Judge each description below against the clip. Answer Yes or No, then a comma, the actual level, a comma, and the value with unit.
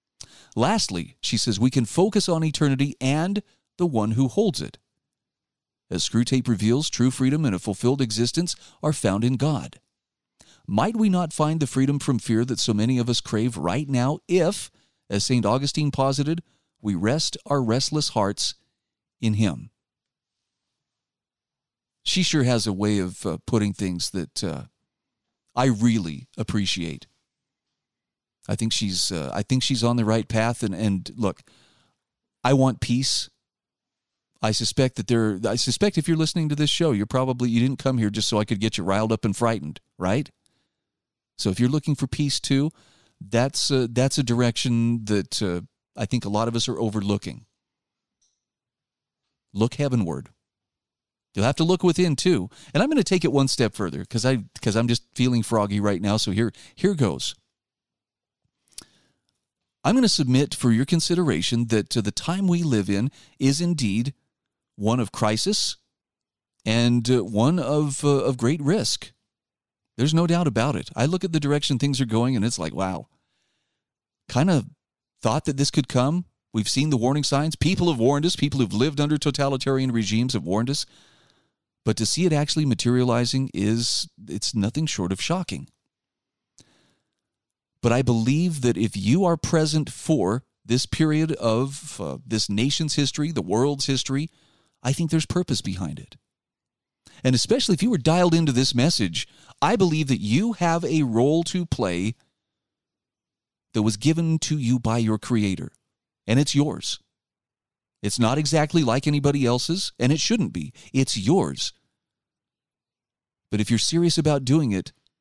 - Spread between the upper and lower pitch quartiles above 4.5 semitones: Yes, average, 5.2 semitones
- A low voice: Yes, low, 125 Hz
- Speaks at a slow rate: No, average, 165 wpm